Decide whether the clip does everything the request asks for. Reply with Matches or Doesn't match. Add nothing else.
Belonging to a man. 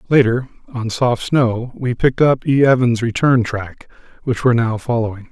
Matches